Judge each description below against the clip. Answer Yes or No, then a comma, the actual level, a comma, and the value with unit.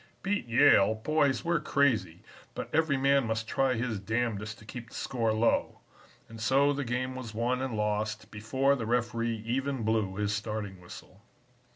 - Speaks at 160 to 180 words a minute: Yes, average, 170 wpm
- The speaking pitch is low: Yes, low, 115 Hz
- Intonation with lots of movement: No, average, 3.6 semitones